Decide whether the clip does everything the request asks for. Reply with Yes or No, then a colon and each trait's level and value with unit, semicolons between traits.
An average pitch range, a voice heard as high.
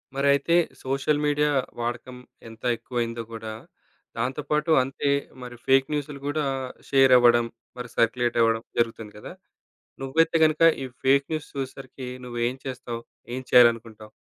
No: average, 3.0 semitones; low, 125 Hz